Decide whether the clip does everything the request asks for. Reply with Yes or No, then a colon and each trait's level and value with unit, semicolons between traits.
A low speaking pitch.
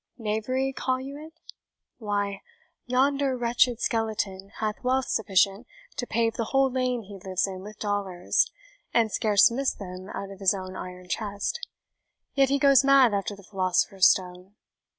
No: high, 215 Hz